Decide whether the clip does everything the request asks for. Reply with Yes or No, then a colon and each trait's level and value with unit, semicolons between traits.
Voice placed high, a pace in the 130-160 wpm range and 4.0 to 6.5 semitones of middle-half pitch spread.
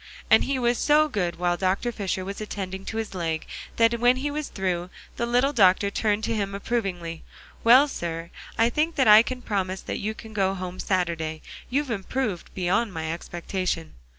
No: high, 200 Hz; average, 185 wpm; average, 4.7 semitones